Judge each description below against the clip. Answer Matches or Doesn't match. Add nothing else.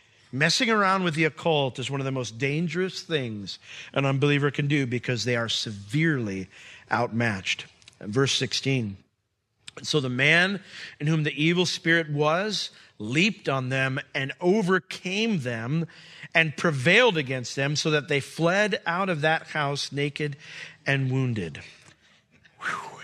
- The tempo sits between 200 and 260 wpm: Doesn't match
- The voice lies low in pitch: Doesn't match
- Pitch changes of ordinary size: Matches